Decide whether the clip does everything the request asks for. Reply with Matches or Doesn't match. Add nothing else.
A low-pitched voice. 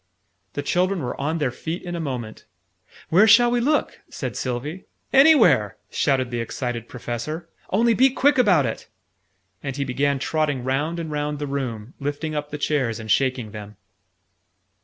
Doesn't match